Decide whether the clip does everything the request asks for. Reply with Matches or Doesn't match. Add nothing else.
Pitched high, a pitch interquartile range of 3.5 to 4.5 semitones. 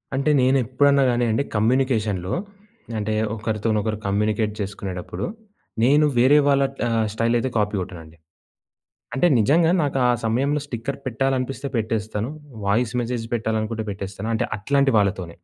Doesn't match